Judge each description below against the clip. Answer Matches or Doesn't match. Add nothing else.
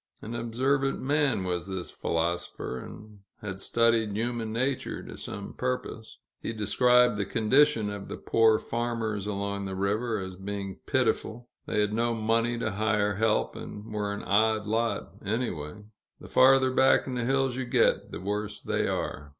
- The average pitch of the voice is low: Matches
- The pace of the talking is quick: Doesn't match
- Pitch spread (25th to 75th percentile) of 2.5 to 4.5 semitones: Matches